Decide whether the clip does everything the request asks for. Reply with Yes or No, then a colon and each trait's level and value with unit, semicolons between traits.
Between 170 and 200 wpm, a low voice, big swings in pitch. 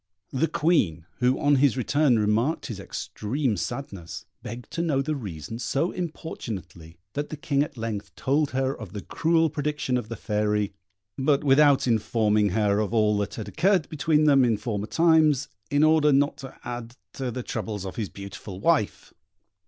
Yes: average, 175 wpm; low, 125 Hz; wide, 5.7 semitones